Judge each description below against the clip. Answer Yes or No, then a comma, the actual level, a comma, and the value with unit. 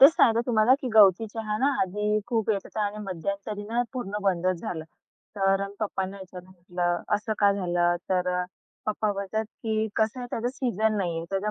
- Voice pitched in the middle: No, high, 205 Hz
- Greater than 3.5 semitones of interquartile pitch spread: No, average, 2.8 semitones